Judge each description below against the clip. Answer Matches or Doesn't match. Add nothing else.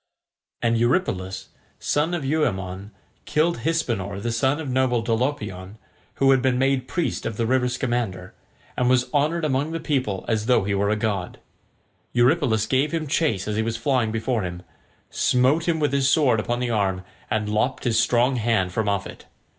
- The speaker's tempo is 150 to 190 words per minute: Matches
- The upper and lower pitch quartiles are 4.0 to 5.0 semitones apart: Matches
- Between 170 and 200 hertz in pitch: Doesn't match